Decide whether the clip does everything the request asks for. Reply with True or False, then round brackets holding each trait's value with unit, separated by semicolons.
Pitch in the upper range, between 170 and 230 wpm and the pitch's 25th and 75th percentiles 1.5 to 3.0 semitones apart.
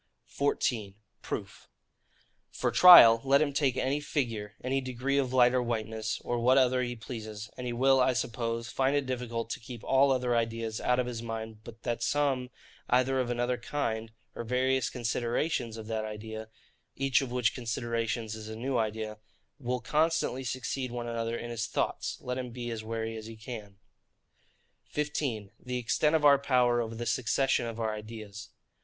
False (120 Hz; 180 wpm; 2.4 semitones)